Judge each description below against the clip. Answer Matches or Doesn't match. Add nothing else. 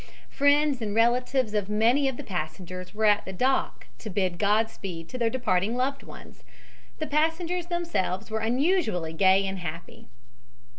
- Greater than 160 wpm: Doesn't match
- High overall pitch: Matches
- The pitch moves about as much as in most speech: Doesn't match